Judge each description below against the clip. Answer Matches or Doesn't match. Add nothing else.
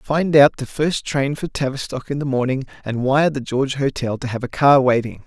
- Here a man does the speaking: Matches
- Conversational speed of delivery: Doesn't match